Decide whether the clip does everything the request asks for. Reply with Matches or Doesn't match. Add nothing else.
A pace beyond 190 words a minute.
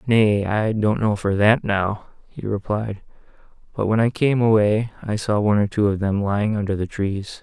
Matches